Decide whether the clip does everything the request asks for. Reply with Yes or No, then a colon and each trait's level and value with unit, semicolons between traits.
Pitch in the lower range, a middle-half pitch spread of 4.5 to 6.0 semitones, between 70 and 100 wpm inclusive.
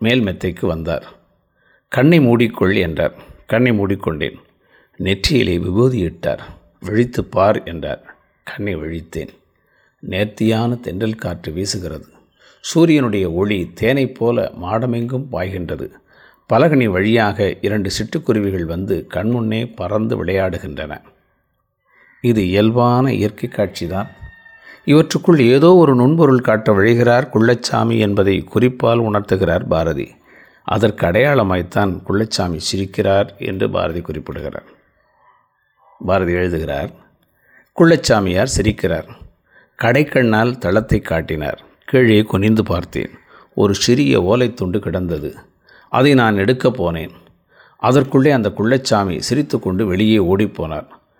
Yes: low, 110 Hz; average, 4.8 semitones; average, 95 wpm